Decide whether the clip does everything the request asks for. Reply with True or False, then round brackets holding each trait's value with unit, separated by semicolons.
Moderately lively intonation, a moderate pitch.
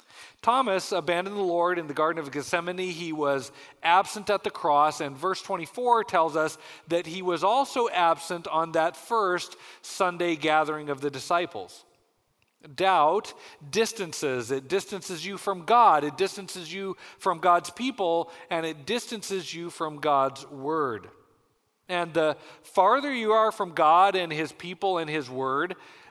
True (3.7 semitones; 175 Hz)